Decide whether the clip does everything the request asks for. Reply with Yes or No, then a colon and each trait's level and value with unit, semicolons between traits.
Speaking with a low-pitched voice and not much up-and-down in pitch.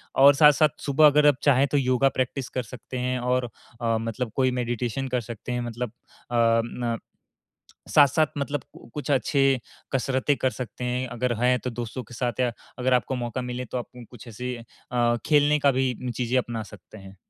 Yes: low, 125 Hz; narrow, 2.0 semitones